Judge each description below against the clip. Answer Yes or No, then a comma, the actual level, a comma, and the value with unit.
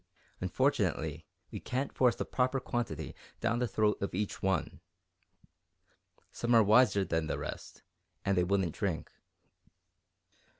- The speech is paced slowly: Yes, slow, 130 wpm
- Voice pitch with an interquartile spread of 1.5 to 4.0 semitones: No, average, 5.1 semitones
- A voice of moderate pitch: No, low, 100 Hz